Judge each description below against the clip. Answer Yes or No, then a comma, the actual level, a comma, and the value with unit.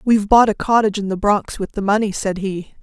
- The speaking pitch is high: Yes, high, 205 Hz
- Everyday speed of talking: No, fast, 255 wpm